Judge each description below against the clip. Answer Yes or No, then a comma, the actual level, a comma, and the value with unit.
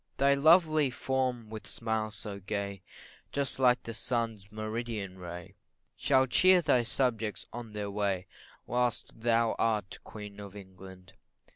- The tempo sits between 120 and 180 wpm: Yes, slow, 135 wpm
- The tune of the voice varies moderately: Yes, average, 3.6 semitones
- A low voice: Yes, low, 110 Hz